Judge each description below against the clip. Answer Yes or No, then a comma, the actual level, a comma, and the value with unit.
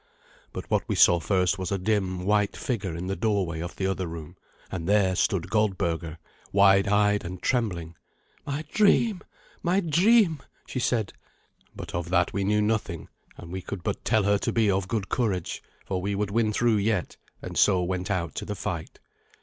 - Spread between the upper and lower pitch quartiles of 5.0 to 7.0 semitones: No, average, 3.1 semitones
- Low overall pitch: Yes, low, 100 Hz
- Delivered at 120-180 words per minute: No, average, 190 wpm